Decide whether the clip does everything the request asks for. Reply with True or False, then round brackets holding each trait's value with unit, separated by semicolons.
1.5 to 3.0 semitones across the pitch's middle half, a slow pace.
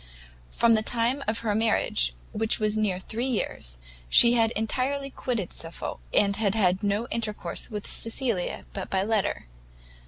False (2.6 semitones; 155 wpm)